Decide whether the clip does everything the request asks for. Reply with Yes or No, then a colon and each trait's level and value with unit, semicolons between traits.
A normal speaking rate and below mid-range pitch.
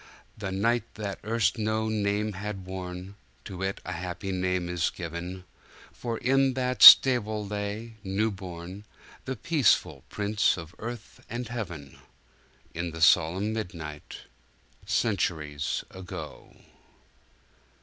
No: slow, 115 wpm; low, 100 Hz